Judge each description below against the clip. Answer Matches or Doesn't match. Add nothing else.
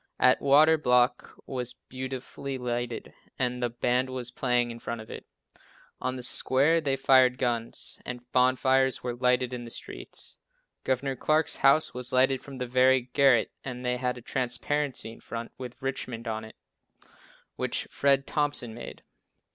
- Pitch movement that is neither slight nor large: Doesn't match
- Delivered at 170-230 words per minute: Doesn't match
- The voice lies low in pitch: Matches